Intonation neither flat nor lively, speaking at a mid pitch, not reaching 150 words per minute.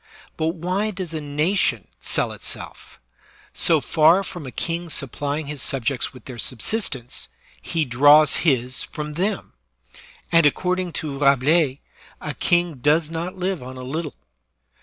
Yes: average, 4.0 semitones; medium, 155 Hz; average, 140 wpm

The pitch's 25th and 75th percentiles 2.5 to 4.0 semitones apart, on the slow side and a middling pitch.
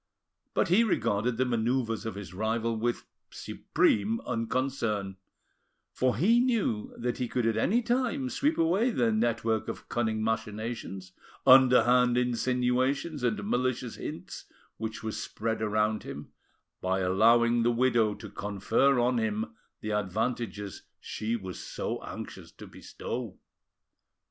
No: average, 2.8 semitones; slow, 130 wpm; low, 115 Hz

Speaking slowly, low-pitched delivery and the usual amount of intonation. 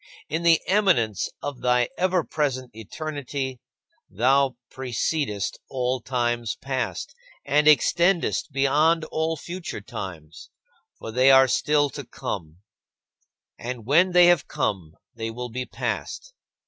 Yes: slow, 120 wpm; low, 130 Hz; average, 4.7 semitones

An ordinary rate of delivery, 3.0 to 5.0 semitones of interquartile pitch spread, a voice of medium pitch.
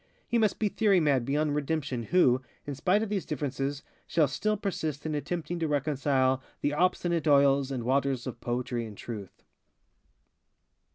Yes: average, 160 wpm; average, 4.5 semitones; medium, 145 Hz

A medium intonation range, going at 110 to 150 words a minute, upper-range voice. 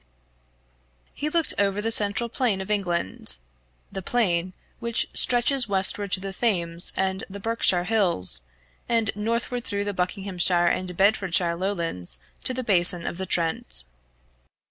Yes: average, 4.1 semitones; average, 140 wpm; high, 195 Hz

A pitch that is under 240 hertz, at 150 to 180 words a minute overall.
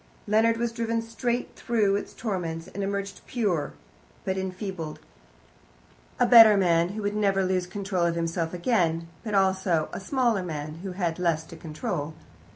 Yes: high, 190 Hz; average, 155 wpm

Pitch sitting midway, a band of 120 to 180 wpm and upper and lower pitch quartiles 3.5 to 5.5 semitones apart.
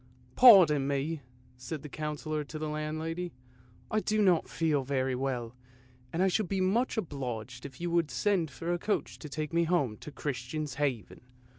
No: medium, 150 Hz; average, 190 wpm; average, 4.4 semitones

